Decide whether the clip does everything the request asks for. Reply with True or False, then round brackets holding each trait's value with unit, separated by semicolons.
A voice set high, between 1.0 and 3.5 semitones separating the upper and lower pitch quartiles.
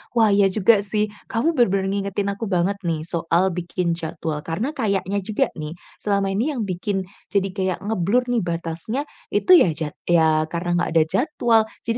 False (195 Hz; 4.0 semitones)